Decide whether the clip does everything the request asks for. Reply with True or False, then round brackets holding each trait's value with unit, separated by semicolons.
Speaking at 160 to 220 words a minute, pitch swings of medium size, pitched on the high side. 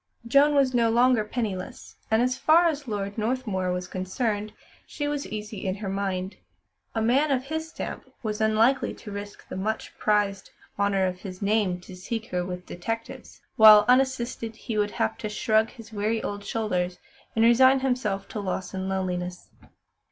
True (175 wpm; 4.0 semitones; 215 Hz)